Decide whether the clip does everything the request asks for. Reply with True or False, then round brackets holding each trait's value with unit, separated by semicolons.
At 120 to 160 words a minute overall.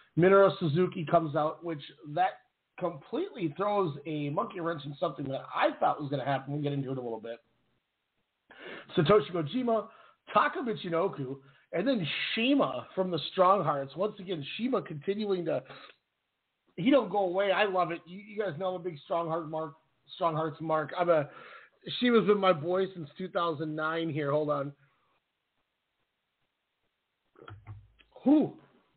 True (155 wpm)